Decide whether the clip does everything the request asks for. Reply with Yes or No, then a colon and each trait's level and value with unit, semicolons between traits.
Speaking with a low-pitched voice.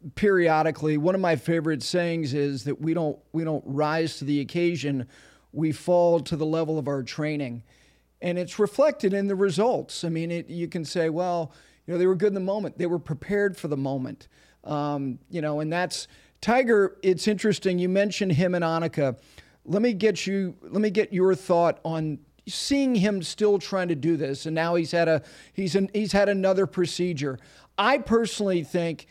No: medium, 170 Hz